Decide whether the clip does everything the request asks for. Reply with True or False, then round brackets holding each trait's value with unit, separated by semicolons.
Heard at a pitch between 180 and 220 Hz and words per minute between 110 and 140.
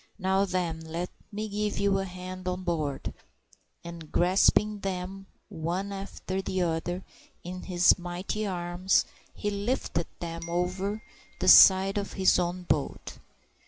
True (185 Hz; 135 wpm)